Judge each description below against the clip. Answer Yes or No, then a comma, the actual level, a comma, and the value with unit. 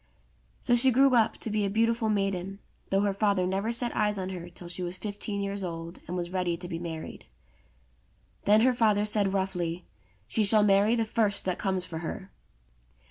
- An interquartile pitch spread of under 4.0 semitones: Yes, average, 3.0 semitones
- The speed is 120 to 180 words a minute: No, average, 195 wpm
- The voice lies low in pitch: No, high, 200 Hz